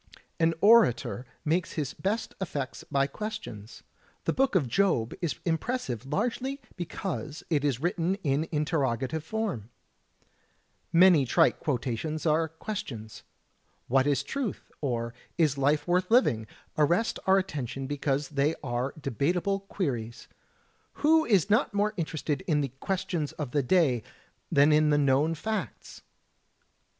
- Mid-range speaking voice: Yes, medium, 155 Hz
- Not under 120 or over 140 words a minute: Yes, slow, 135 wpm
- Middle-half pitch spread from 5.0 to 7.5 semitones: Yes, wide, 5.5 semitones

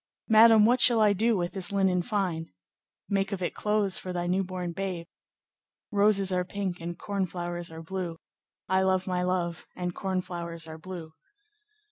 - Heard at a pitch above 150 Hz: Yes, medium, 185 Hz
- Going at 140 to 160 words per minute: No, average, 170 wpm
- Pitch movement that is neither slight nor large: No, narrow, 2.3 semitones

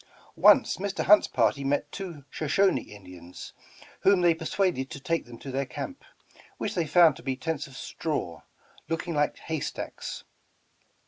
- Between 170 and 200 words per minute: No, average, 150 wpm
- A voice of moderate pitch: Yes, medium, 150 Hz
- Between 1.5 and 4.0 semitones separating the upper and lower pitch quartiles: No, average, 4.6 semitones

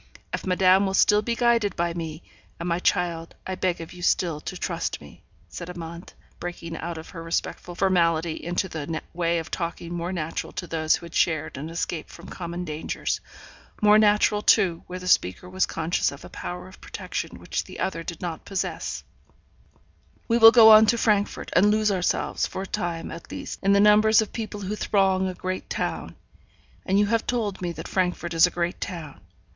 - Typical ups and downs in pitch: Yes, average, 3.1 semitones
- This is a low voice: No, medium, 180 Hz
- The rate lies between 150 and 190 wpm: No, average, 200 wpm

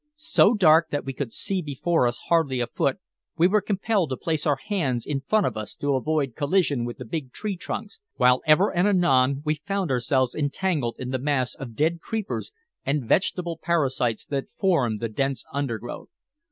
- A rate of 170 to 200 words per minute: Yes, average, 190 wpm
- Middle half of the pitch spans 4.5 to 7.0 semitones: Yes, average, 5.2 semitones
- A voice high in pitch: No, medium, 145 Hz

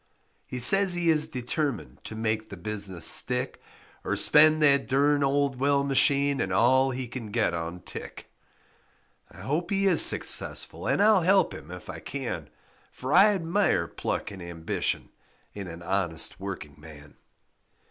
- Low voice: Yes, low, 125 Hz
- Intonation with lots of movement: Yes, wide, 8.0 semitones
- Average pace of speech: Yes, average, 155 wpm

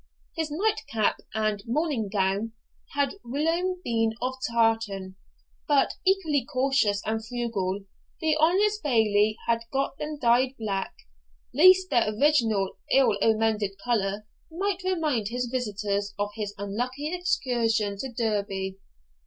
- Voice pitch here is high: Yes, high, 235 Hz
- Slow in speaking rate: Yes, slow, 125 wpm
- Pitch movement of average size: No, wide, 5.9 semitones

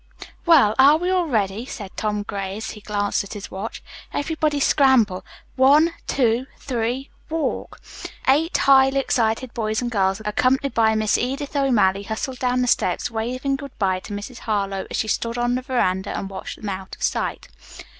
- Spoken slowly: No, average, 175 wpm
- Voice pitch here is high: Yes, high, 235 Hz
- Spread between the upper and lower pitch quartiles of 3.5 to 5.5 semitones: Yes, average, 4.7 semitones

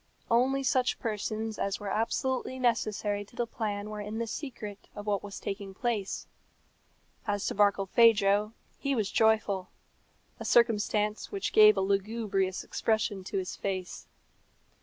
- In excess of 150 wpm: No, average, 140 wpm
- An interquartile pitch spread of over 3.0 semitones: No, narrow, 2.5 semitones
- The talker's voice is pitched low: No, high, 210 Hz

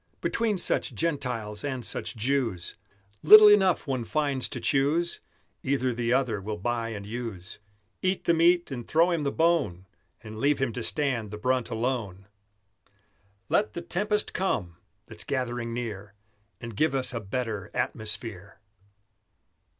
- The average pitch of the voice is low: Yes, low, 125 Hz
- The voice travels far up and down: Yes, wide, 5.9 semitones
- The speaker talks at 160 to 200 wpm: No, average, 145 wpm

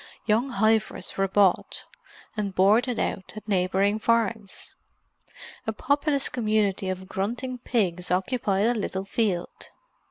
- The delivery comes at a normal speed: No, slow, 120 wpm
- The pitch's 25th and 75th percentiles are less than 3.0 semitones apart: No, average, 3.3 semitones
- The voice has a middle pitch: No, high, 210 Hz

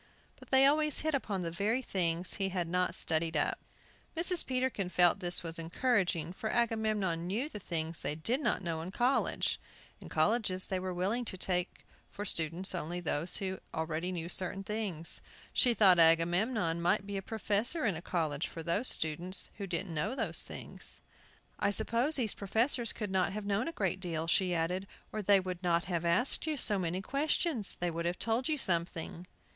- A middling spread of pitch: Yes, average, 4.5 semitones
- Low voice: No, medium, 185 Hz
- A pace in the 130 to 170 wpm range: No, average, 190 wpm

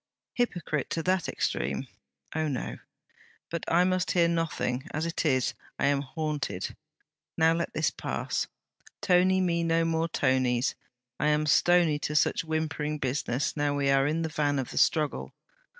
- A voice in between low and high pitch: Yes, medium, 155 Hz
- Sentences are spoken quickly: No, average, 155 wpm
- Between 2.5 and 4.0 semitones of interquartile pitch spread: Yes, average, 2.8 semitones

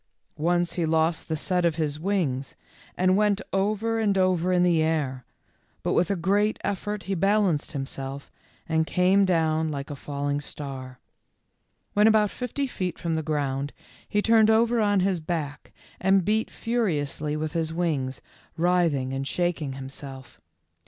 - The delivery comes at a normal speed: Yes, average, 160 wpm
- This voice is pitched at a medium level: Yes, medium, 170 Hz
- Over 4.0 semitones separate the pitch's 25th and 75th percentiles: Yes, average, 5.1 semitones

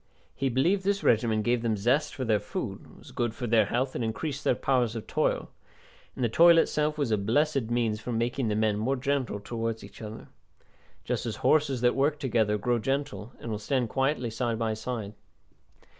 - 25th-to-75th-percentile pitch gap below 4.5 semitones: Yes, average, 3.7 semitones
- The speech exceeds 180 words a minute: Yes, average, 200 wpm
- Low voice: Yes, low, 120 Hz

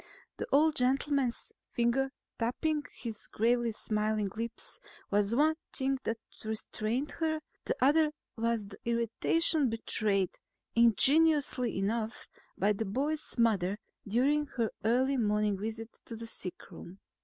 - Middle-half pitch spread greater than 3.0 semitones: Yes, average, 4.1 semitones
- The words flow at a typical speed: No, slow, 120 wpm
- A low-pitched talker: No, high, 235 Hz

